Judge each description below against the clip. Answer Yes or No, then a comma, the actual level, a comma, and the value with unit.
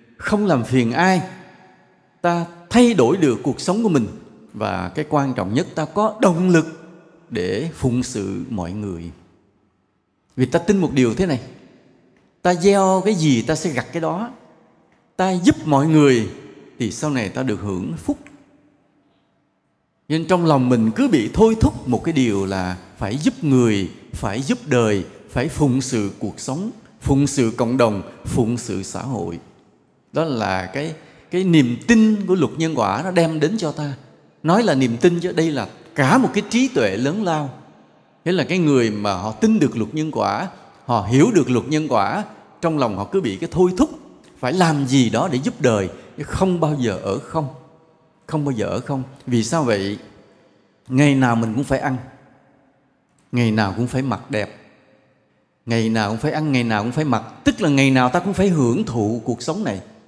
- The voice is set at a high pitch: No, medium, 140 Hz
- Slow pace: No, average, 190 wpm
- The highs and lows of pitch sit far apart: Yes, wide, 6.5 semitones